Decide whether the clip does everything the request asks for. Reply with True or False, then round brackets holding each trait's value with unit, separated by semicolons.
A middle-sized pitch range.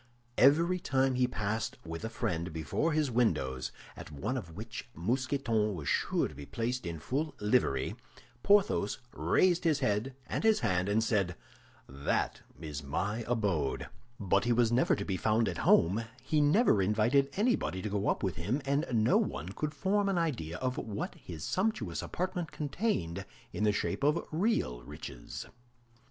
False (8.2 semitones)